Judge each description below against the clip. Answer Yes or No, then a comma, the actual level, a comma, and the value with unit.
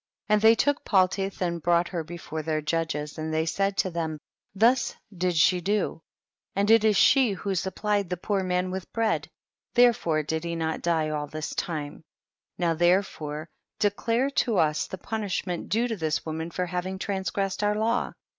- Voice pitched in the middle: Yes, medium, 180 Hz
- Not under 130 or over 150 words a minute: No, average, 185 wpm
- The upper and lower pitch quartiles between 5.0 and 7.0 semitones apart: No, average, 4.2 semitones